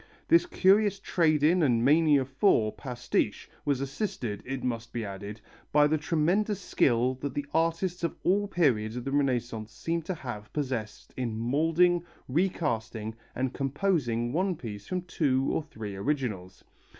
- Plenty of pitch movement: Yes, wide, 6.1 semitones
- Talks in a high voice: No, medium, 140 Hz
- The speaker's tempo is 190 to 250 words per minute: No, average, 150 wpm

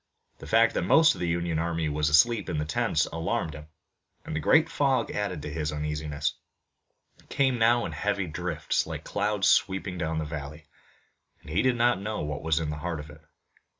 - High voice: No, very low, 85 Hz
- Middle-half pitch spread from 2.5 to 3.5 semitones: No, average, 5.3 semitones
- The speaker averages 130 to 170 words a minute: No, fast, 205 wpm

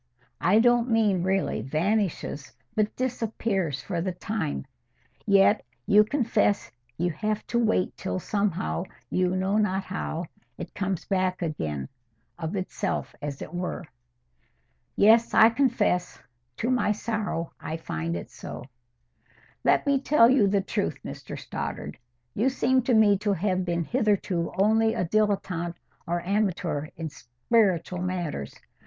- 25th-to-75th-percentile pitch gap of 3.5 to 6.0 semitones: Yes, average, 4.3 semitones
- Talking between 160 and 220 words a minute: No, slow, 135 wpm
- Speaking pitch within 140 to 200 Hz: Yes, high, 190 Hz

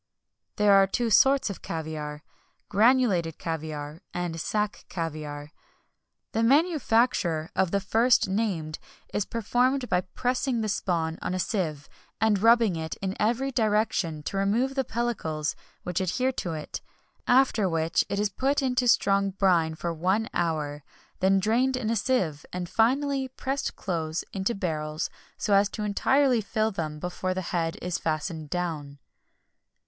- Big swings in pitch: Yes, wide, 6.0 semitones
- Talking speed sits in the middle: Yes, average, 155 wpm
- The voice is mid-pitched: No, high, 195 Hz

